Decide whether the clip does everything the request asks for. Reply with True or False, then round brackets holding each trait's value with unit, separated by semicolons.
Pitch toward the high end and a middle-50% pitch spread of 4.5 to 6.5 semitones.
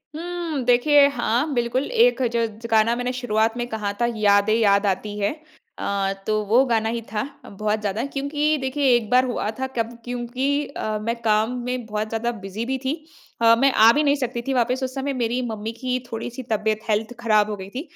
False (235 Hz; 3.2 semitones)